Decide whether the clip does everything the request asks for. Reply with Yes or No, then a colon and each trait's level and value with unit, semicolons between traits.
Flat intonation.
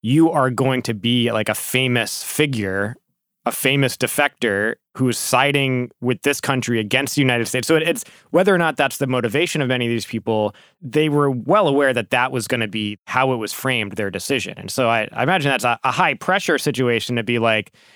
No: average, 3.2 semitones